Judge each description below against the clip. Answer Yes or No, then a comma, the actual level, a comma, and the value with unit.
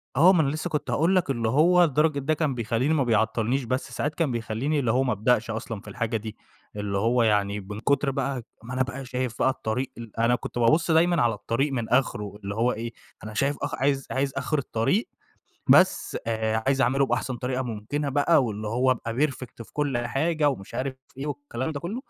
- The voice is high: No, low, 130 Hz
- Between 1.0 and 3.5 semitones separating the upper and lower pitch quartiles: No, average, 3.9 semitones